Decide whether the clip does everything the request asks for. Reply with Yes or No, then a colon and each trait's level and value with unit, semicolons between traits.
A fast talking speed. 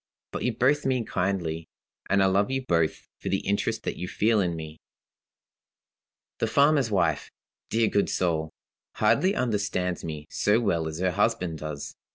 No: average, 165 wpm